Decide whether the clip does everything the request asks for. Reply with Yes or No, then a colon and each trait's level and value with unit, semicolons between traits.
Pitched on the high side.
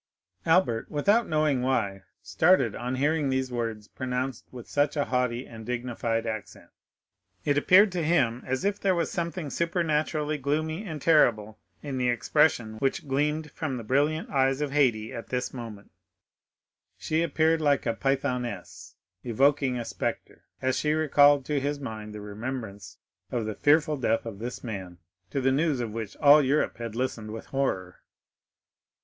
No: low, 130 Hz